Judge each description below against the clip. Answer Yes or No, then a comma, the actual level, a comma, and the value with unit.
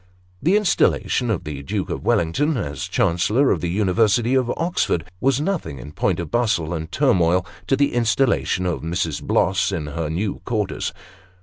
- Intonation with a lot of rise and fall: Yes, wide, 7.2 semitones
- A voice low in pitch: Yes, very low, 95 Hz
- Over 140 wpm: Yes, average, 170 wpm